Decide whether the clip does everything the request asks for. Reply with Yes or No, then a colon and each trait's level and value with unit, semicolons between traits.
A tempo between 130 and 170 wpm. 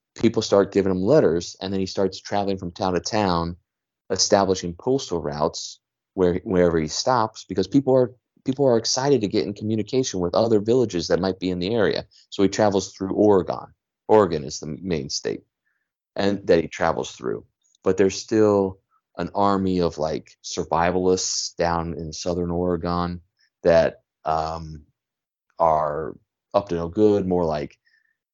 Yes: average, 160 wpm